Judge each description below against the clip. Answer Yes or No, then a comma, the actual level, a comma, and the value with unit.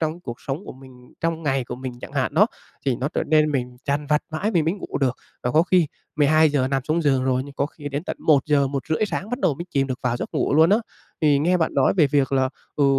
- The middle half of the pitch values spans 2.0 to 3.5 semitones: Yes, average, 3.1 semitones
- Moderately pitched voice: Yes, medium, 145 Hz